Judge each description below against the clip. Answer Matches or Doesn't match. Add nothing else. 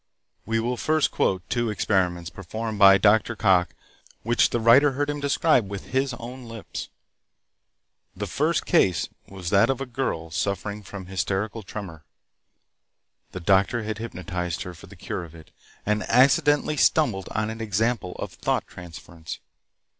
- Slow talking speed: Doesn't match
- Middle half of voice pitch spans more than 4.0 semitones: Matches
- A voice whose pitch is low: Matches